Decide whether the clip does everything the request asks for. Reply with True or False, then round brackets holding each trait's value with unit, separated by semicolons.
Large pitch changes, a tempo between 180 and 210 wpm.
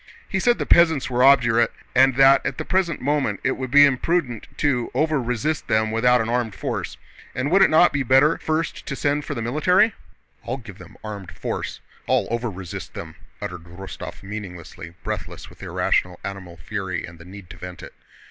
True (6.5 semitones; 185 wpm)